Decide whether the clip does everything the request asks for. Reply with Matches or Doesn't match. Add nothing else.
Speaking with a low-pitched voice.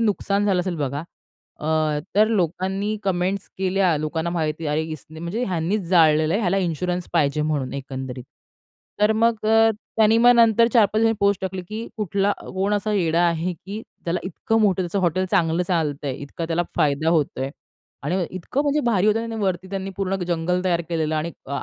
Doesn't match